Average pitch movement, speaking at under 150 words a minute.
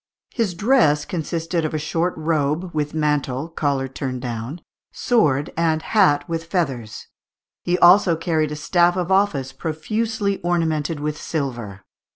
Yes: average, 3.3 semitones; average, 140 wpm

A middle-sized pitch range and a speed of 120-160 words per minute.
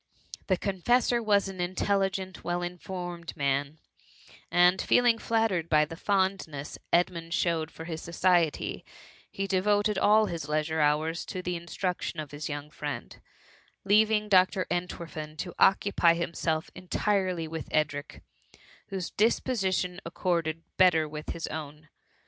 Yes: average, 3.4 semitones; average, 140 wpm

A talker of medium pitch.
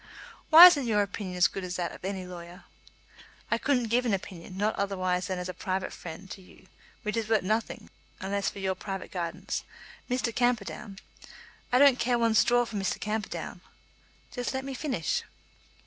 No: high, 200 Hz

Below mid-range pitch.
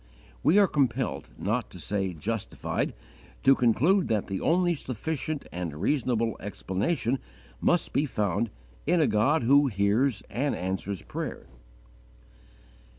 Yes: low, 125 Hz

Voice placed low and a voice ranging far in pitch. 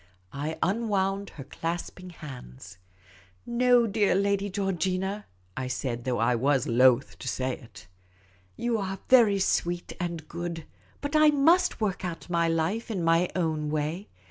No: medium, 175 Hz; wide, 7.0 semitones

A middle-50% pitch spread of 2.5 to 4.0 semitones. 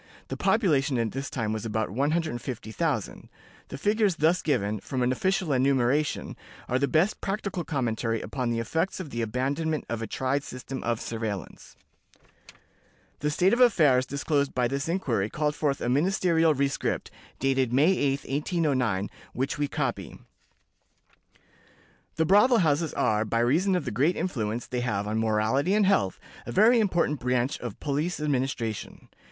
No: average, 5.3 semitones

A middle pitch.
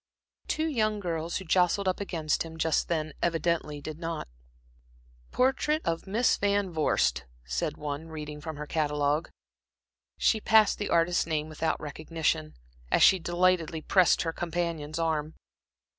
Yes: medium, 165 Hz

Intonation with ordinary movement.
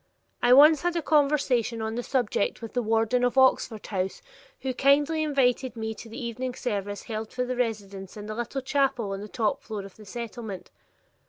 Yes: average, 3.4 semitones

